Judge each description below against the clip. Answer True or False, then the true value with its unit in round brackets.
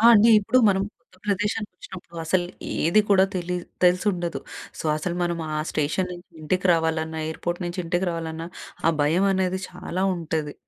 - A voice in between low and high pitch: True (175 Hz)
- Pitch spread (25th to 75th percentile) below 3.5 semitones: True (2.4 semitones)